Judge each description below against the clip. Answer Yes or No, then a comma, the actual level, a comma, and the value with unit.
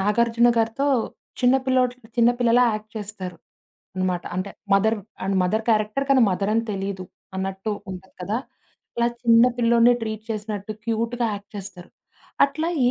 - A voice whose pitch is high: Yes, high, 220 Hz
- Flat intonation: No, average, 3.2 semitones